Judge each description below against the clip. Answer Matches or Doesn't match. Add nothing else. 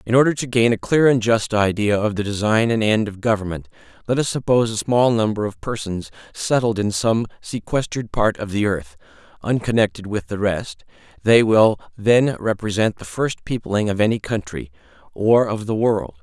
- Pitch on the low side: Matches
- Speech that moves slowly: Doesn't match